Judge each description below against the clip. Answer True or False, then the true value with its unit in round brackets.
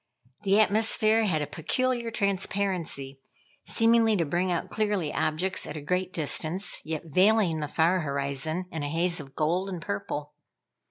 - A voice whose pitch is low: False (175 Hz)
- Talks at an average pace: True (155 wpm)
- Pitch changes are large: False (4.8 semitones)